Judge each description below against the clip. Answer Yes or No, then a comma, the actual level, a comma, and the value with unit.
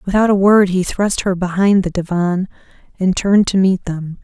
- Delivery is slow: No, average, 200 wpm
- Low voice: No, high, 190 Hz